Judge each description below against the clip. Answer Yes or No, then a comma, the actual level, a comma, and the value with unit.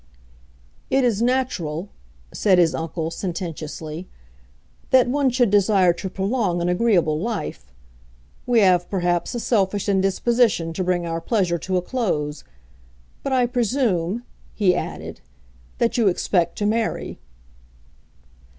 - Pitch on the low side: No, high, 190 Hz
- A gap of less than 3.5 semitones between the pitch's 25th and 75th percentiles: No, wide, 5.4 semitones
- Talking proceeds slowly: Yes, slow, 125 wpm